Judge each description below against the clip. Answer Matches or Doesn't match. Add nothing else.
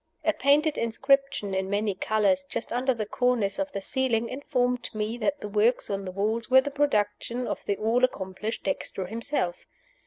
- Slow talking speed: Doesn't match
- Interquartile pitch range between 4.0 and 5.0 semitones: Matches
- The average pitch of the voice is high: Matches